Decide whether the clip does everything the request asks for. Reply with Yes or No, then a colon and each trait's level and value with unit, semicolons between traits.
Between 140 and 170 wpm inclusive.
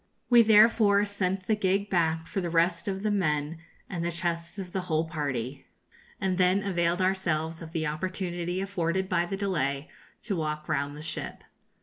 No: average, 180 wpm